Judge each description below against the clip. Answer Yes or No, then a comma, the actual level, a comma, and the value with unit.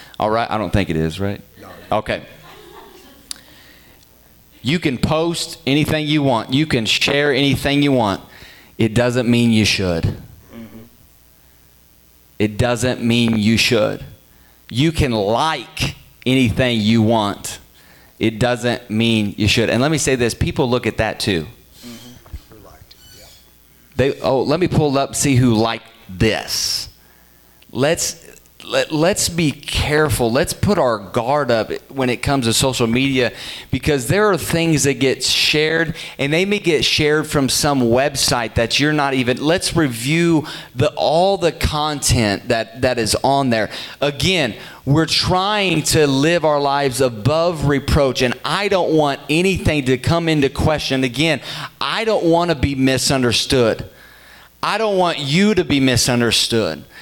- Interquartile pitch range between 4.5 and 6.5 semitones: Yes, average, 5.1 semitones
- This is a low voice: Yes, low, 130 Hz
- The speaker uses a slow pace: No, average, 145 wpm